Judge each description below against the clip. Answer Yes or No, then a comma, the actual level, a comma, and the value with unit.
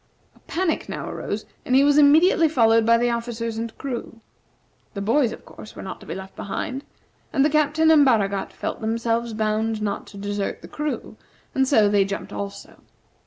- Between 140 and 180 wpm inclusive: No, average, 190 wpm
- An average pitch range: Yes, average, 5.0 semitones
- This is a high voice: Yes, high, 230 Hz